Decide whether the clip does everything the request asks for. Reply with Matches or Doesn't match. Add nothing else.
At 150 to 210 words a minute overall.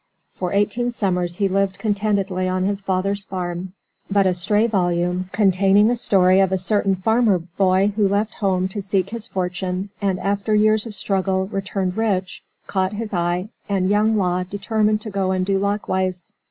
Matches